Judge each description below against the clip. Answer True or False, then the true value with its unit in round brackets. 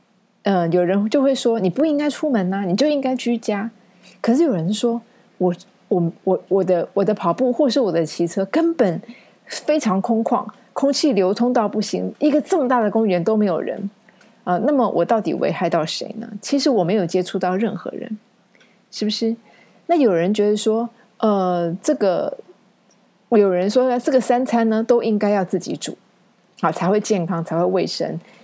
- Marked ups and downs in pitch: False (4.6 semitones)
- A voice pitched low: False (215 Hz)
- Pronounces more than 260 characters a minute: True (270 characters per minute)